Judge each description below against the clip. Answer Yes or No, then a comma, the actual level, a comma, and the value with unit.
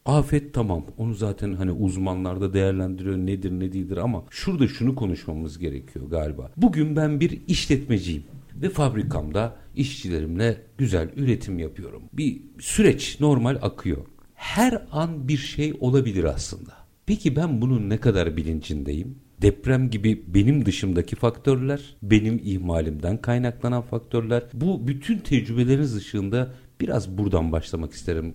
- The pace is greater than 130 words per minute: No, average, 125 wpm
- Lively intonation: Yes, wide, 6.6 semitones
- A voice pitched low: Yes, low, 115 Hz